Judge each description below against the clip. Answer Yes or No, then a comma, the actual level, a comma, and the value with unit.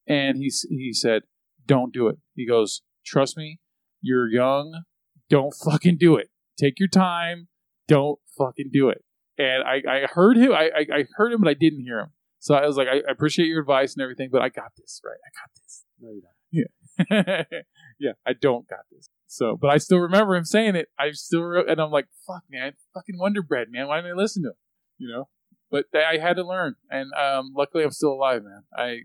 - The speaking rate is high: Yes, fast, 215 wpm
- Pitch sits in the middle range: Yes, medium, 150 Hz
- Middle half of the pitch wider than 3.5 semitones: Yes, average, 4.6 semitones